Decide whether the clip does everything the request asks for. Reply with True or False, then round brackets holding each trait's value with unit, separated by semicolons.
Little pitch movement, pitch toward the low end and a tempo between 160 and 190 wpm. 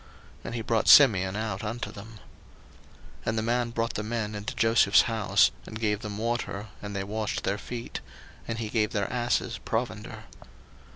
True (2.0 semitones; 110 Hz; 175 wpm)